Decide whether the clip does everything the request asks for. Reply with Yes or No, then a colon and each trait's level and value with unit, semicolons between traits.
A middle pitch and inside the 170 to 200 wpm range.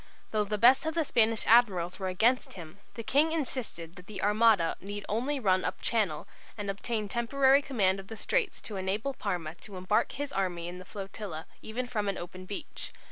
No: high, 210 Hz; average, 195 wpm